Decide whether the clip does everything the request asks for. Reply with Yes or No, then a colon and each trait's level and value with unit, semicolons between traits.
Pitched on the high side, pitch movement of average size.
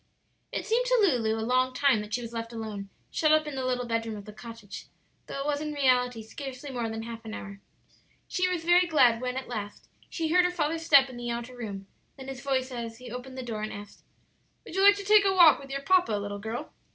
Yes: very high, 250 Hz; average, 4.9 semitones